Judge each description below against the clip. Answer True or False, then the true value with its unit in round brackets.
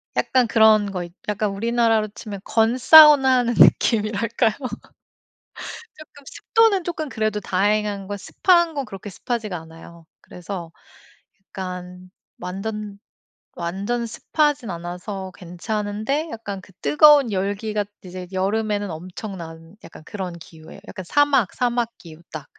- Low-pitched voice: False (210 Hz)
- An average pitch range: True (4.4 semitones)